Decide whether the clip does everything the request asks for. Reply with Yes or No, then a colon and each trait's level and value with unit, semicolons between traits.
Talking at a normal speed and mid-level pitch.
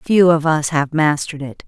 No: fast, 215 wpm; medium, 155 Hz